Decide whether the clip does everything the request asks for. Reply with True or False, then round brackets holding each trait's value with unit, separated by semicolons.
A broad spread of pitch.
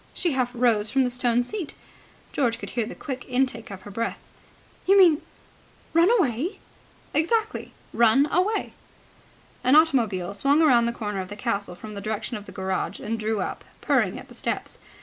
True (5.7 semitones)